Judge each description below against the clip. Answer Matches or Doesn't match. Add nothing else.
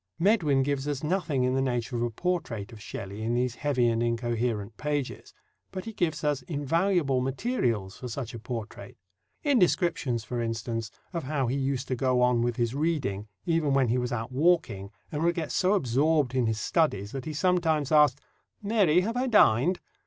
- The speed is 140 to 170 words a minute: Doesn't match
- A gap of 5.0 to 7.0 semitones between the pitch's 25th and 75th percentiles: Matches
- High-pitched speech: Doesn't match